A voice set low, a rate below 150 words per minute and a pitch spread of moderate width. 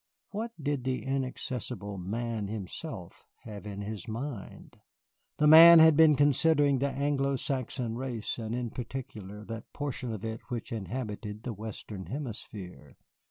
Yes: low, 120 Hz; average, 140 wpm; average, 4.7 semitones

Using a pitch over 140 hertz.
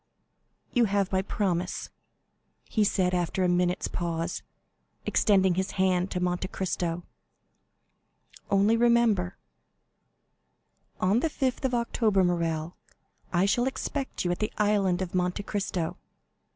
Yes: high, 190 Hz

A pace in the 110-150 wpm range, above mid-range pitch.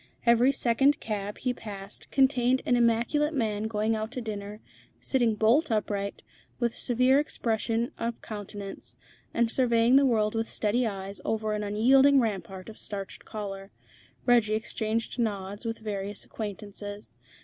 Yes: average, 145 wpm; high, 220 Hz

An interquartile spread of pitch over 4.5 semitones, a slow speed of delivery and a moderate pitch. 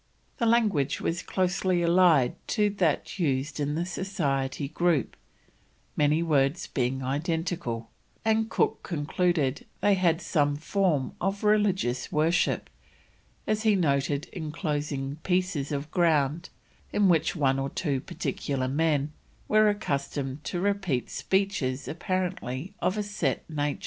Yes: average, 4.9 semitones; slow, 125 wpm; medium, 160 Hz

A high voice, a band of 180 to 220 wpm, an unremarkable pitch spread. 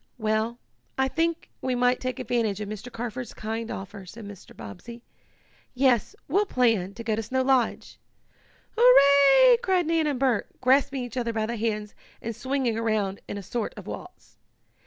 No: high, 240 Hz; average, 170 wpm; average, 3.5 semitones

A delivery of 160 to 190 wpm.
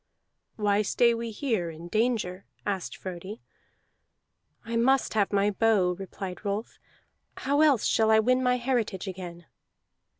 No: slow, 135 wpm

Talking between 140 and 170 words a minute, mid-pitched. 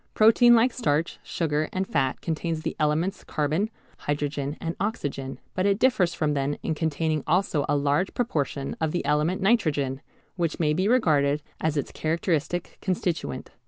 Yes: average, 160 wpm; medium, 160 Hz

